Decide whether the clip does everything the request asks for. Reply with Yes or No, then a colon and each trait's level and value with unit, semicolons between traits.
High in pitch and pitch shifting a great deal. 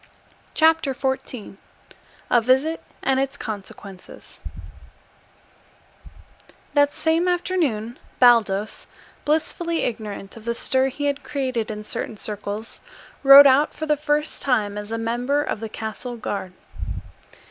No: very high, 250 Hz; average, 4.9 semitones